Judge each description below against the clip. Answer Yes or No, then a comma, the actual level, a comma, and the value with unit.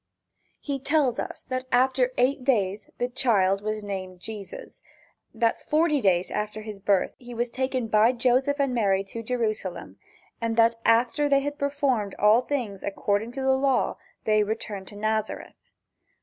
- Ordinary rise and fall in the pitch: Yes, average, 3.9 semitones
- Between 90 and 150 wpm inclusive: No, average, 160 wpm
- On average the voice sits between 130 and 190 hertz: No, high, 230 Hz